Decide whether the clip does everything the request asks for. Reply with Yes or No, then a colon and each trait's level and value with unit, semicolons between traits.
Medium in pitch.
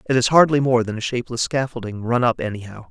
No: low, 120 Hz